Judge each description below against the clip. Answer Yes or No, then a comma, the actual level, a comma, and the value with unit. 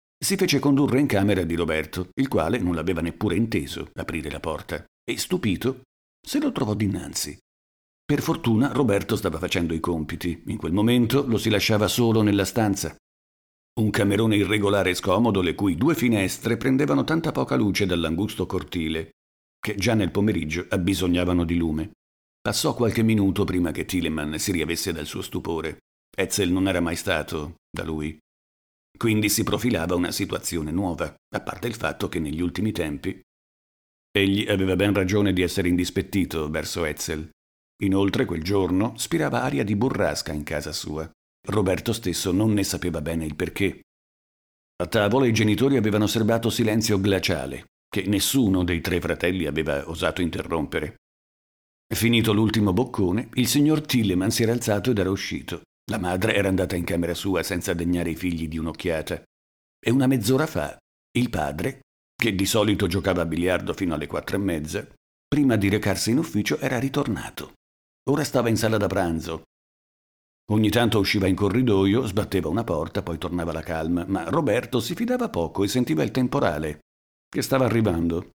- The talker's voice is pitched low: Yes, very low, 95 Hz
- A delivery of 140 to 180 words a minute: Yes, average, 165 wpm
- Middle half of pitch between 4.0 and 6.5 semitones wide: Yes, average, 5.0 semitones